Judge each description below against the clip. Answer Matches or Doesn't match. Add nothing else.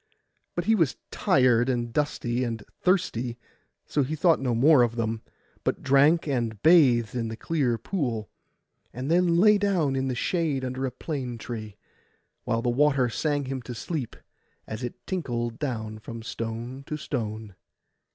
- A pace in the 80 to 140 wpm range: Doesn't match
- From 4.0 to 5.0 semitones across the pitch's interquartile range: Matches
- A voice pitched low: Matches